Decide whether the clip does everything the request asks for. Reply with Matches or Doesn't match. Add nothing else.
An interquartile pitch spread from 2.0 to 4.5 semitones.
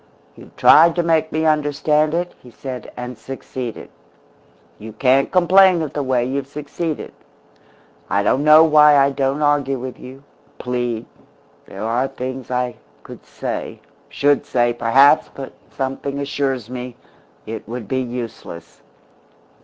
Matches